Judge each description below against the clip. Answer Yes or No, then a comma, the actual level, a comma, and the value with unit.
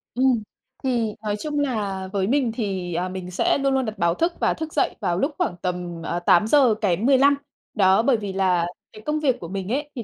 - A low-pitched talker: No, high, 215 Hz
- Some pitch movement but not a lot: No, wide, 6.1 semitones